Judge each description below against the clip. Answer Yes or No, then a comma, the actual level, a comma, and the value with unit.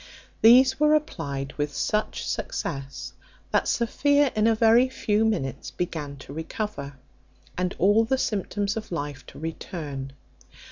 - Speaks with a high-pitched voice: Yes, high, 205 Hz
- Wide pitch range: Yes, wide, 7.8 semitones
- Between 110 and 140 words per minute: Yes, slow, 135 wpm